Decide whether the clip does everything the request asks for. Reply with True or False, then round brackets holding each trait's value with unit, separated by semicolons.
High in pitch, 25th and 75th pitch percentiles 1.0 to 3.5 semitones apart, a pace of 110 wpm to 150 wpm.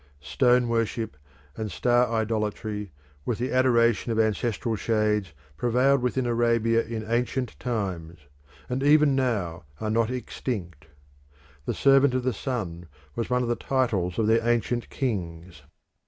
False (115 Hz; 2.9 semitones; 140 wpm)